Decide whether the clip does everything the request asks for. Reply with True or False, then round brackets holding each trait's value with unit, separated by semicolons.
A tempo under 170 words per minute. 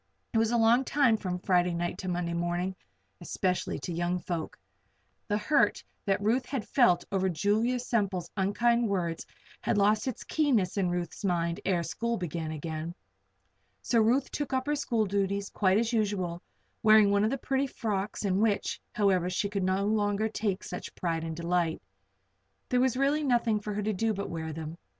False (180 wpm)